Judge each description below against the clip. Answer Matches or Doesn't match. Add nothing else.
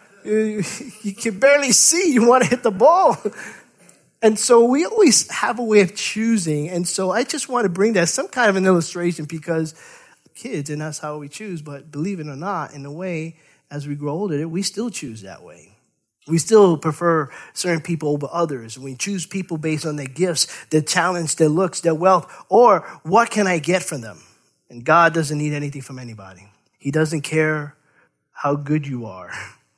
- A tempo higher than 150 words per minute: Matches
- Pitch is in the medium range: Matches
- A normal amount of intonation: Doesn't match